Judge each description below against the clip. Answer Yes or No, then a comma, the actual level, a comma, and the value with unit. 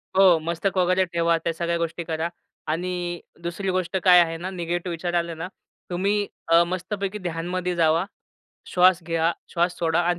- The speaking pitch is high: No, medium, 175 Hz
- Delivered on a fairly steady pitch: Yes, narrow, 1.5 semitones